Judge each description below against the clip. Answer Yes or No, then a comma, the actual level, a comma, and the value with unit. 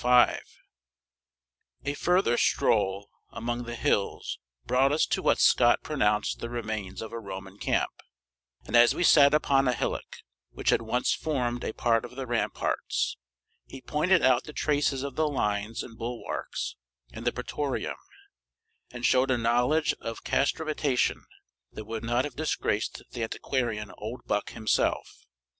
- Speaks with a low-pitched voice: Yes, low, 120 Hz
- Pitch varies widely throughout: No, average, 3.7 semitones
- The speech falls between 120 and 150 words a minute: Yes, average, 145 wpm